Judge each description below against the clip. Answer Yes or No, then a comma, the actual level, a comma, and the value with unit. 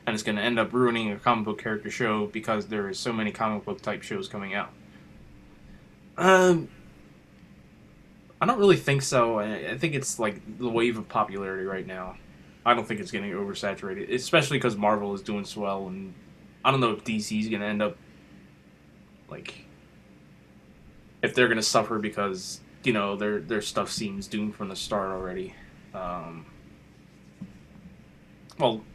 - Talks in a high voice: No, low, 110 Hz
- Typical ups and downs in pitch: Yes, average, 3.6 semitones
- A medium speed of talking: Yes, average, 170 wpm